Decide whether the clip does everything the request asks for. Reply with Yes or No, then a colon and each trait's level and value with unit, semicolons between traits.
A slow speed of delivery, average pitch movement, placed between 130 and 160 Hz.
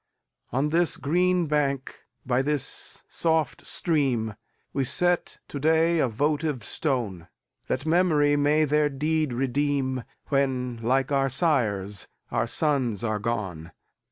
Yes: slow, 110 wpm; average, 3.9 semitones; medium, 140 Hz